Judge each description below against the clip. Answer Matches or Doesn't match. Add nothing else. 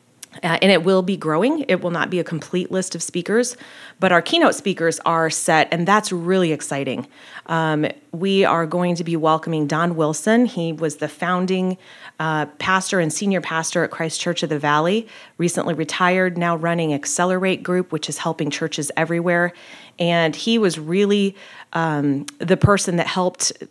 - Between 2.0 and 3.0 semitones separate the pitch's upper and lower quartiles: Matches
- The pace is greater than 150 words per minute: Matches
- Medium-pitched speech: Matches